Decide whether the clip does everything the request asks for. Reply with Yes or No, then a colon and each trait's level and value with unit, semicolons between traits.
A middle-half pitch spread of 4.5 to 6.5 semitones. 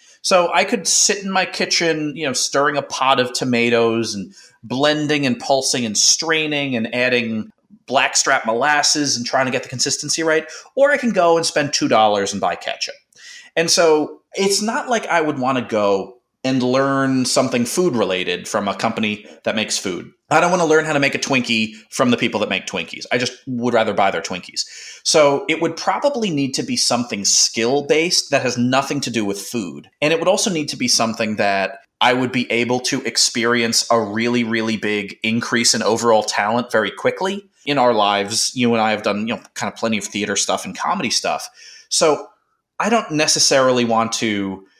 Yes: wide, 5.6 semitones